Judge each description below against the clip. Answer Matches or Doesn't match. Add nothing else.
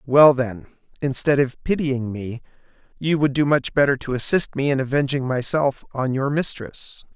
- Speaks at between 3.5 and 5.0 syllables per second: Matches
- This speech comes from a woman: Doesn't match